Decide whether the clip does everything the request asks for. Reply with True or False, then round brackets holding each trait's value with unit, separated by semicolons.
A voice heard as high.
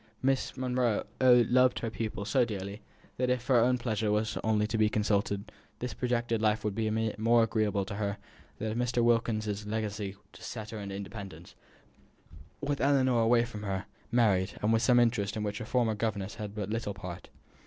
False (110 Hz)